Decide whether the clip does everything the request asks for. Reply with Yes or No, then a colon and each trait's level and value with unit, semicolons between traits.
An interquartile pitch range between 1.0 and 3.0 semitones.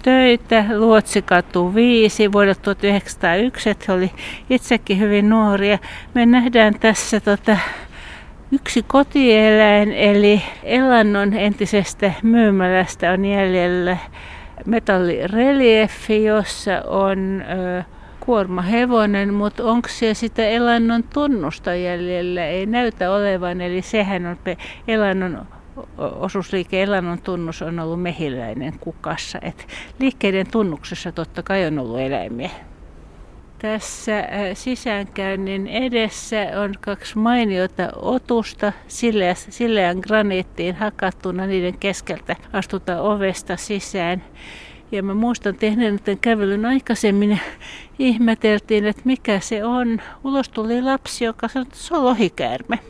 No: average, 3.5 semitones